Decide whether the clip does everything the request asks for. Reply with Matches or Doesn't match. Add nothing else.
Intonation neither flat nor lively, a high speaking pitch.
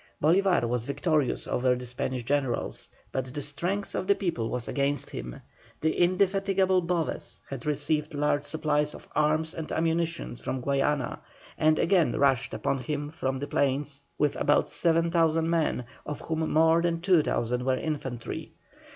Doesn't match